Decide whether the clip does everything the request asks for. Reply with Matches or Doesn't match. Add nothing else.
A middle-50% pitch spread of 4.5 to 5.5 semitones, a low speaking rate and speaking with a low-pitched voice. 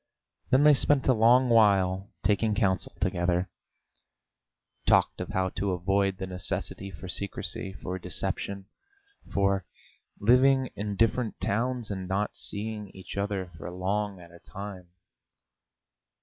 Doesn't match